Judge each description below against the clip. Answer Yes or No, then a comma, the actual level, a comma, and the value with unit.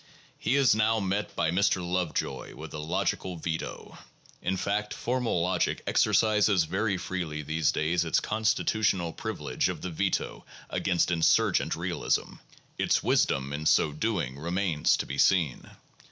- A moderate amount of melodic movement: Yes, average, 4.4 semitones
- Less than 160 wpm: Yes, average, 140 wpm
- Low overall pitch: Yes, very low, 90 Hz